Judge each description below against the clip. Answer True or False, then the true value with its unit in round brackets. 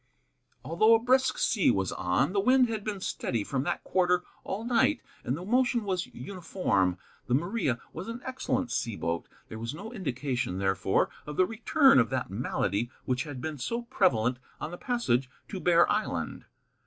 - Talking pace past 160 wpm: True (180 wpm)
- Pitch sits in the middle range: True (175 Hz)